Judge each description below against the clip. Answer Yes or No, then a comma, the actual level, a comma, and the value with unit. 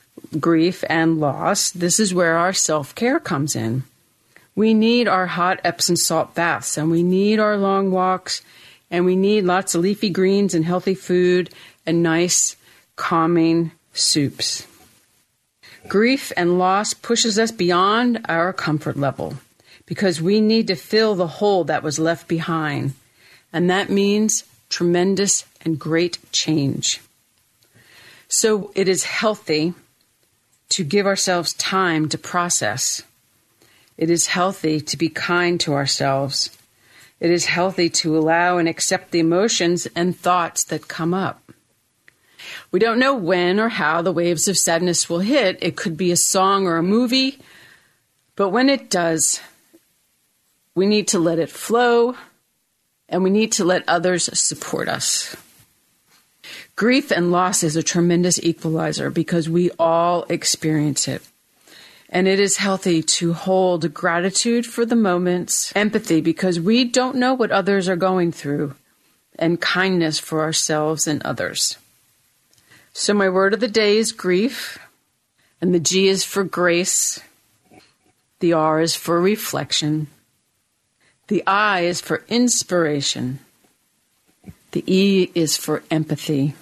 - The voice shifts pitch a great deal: No, average, 3.3 semitones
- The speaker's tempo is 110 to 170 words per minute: Yes, average, 140 wpm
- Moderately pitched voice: Yes, medium, 175 Hz